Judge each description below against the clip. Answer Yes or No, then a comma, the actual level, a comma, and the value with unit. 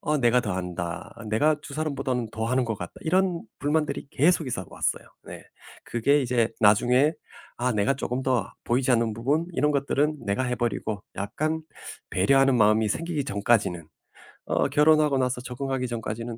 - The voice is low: Yes, low, 125 Hz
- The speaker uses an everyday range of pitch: Yes, average, 4.6 semitones